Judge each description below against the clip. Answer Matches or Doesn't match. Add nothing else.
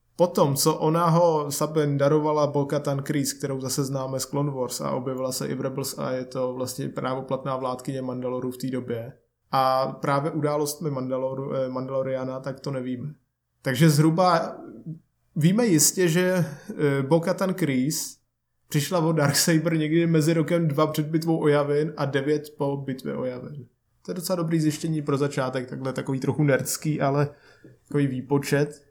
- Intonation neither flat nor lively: Matches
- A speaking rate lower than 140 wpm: Doesn't match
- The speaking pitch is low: Doesn't match